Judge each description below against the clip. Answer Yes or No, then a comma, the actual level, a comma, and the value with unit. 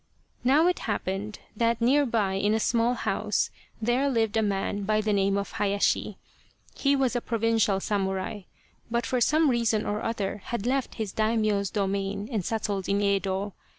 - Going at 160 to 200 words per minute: Yes, average, 170 wpm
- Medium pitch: No, high, 215 Hz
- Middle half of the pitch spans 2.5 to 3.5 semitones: Yes, average, 2.9 semitones